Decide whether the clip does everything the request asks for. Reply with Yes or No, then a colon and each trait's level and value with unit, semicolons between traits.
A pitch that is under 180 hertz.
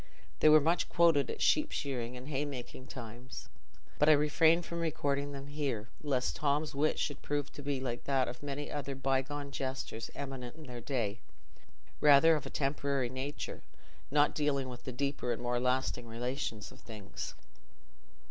Yes: medium, 140 Hz